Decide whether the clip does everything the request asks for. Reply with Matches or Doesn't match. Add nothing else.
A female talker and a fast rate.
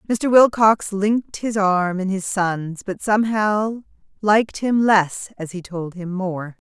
Doesn't match